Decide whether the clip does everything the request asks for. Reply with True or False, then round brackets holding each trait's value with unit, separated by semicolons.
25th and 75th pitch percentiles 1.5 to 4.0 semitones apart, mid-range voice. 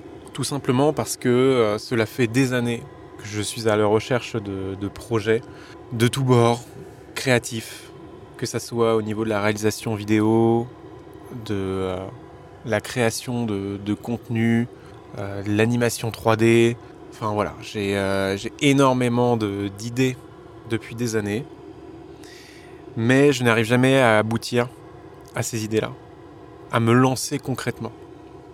False (2.9 semitones; 115 Hz)